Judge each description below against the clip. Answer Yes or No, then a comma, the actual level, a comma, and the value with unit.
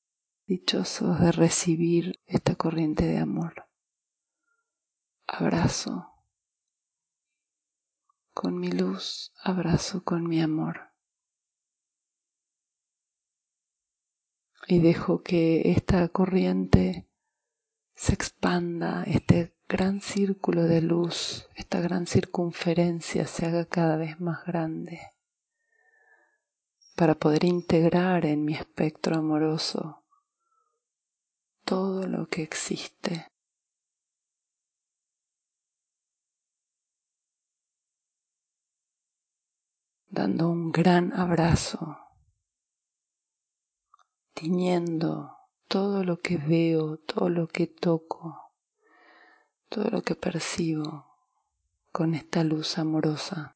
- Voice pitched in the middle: Yes, medium, 170 Hz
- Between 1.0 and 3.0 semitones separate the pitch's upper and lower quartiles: Yes, narrow, 2.4 semitones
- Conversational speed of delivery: No, slow, 75 wpm